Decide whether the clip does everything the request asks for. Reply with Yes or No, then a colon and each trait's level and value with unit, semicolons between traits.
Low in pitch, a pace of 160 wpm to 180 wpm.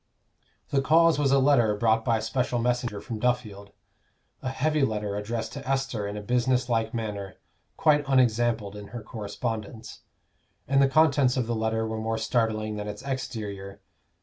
Yes: low, 115 Hz; average, 170 wpm